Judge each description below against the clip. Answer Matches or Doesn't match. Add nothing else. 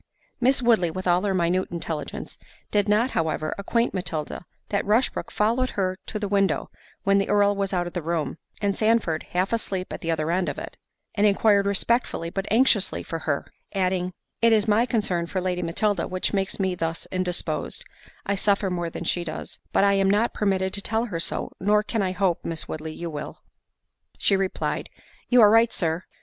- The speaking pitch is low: Doesn't match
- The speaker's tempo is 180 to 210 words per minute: Matches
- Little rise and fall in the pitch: Doesn't match